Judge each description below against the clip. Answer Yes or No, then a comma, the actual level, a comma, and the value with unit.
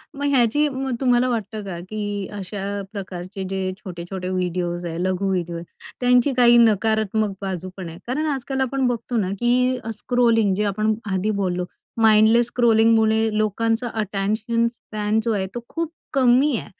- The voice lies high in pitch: Yes, high, 220 Hz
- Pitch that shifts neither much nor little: Yes, average, 4.1 semitones